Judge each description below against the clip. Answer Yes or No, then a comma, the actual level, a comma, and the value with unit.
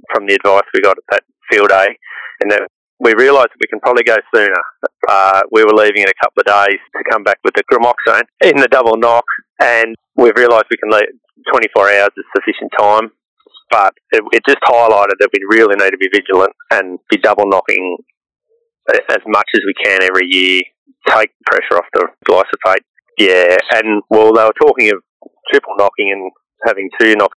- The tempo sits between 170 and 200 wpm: Yes, average, 195 wpm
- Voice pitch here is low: Yes, low, 110 Hz